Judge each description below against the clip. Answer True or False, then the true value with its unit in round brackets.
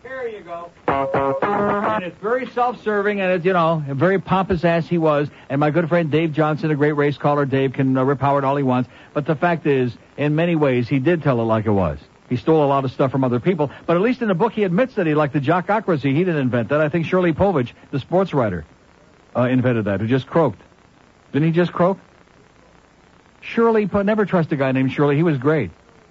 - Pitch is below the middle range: False (155 Hz)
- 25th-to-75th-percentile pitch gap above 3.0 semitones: True (4.8 semitones)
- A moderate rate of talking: False (235 wpm)